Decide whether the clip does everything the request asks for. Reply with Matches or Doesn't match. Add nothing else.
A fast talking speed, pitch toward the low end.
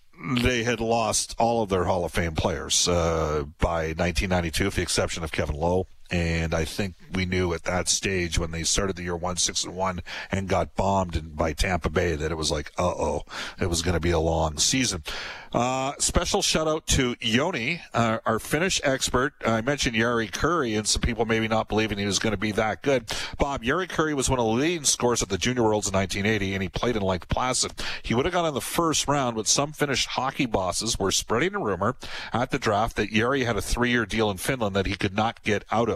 Matches